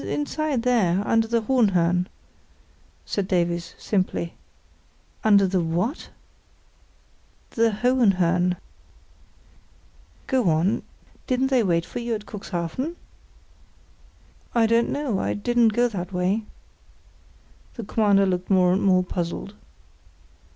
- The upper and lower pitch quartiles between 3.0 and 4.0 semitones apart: No, average, 4.6 semitones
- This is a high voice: Yes, high, 200 Hz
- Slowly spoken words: Yes, slow, 105 wpm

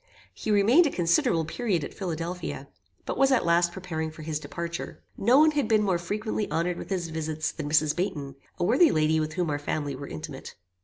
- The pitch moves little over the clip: No, average, 4.6 semitones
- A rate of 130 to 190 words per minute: No, fast, 205 wpm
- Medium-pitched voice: Yes, medium, 170 Hz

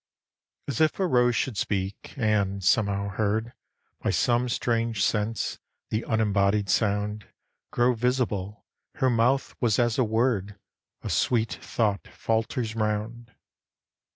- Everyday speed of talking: No, slow, 125 wpm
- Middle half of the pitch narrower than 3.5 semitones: Yes, narrow, 2.6 semitones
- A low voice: Yes, low, 110 Hz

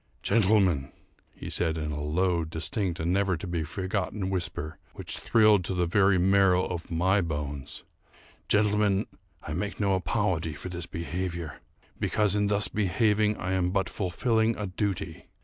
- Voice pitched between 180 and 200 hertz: No, very low, 95 Hz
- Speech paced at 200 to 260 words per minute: No, average, 155 wpm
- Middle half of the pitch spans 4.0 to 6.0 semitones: No, average, 3.4 semitones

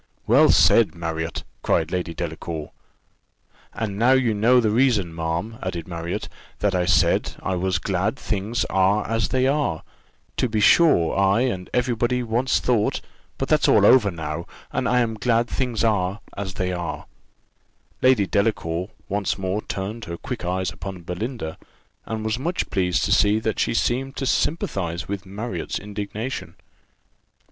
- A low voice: Yes, low, 100 Hz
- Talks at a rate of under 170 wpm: Yes, average, 160 wpm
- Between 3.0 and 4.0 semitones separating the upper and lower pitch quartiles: No, average, 4.6 semitones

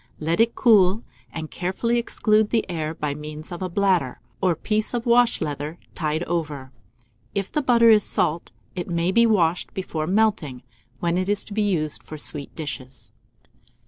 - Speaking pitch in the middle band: Yes, medium, 175 Hz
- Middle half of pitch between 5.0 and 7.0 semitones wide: Yes, wide, 5.5 semitones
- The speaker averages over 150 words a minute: Yes, average, 175 wpm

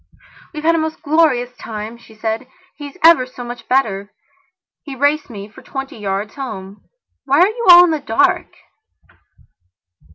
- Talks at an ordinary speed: Yes, average, 160 wpm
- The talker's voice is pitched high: Yes, very high, 260 Hz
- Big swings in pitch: Yes, wide, 5.8 semitones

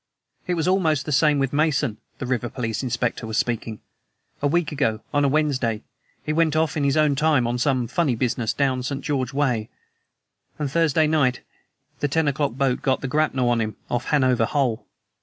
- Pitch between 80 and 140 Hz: Yes, low, 135 Hz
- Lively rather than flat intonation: No, average, 3.6 semitones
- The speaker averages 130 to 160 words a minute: No, average, 195 wpm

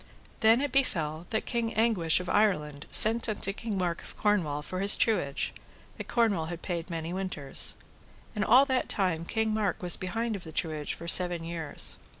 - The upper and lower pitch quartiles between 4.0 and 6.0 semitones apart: Yes, average, 5.0 semitones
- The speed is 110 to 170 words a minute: No, average, 180 wpm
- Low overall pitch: No, medium, 185 Hz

